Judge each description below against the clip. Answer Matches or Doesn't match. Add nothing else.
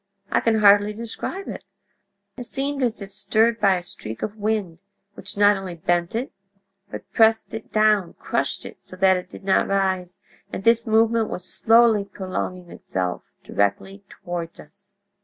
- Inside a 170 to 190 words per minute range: Doesn't match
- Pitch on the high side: Matches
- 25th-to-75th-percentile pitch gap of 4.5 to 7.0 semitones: Doesn't match